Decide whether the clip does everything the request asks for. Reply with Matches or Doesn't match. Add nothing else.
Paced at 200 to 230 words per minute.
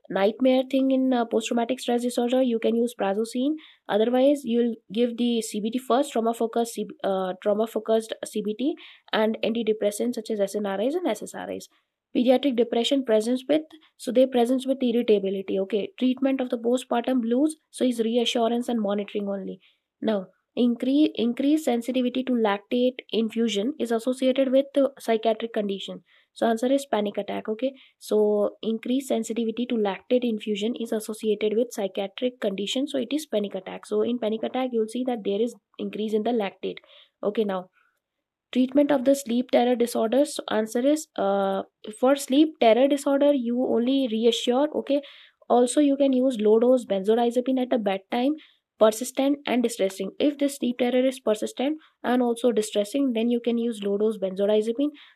Doesn't match